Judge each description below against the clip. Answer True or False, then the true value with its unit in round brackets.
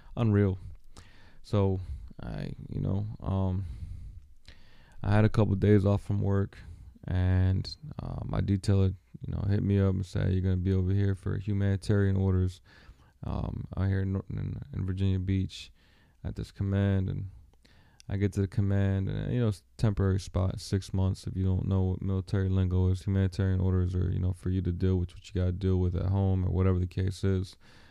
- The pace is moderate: True (195 wpm)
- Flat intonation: True (1.3 semitones)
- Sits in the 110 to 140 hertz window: False (95 Hz)